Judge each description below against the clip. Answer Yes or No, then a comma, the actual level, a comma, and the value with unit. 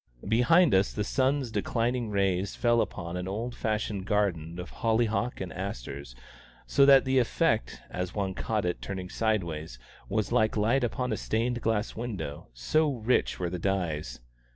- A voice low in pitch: Yes, low, 105 Hz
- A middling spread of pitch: Yes, average, 4.8 semitones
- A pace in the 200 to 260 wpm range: No, average, 165 wpm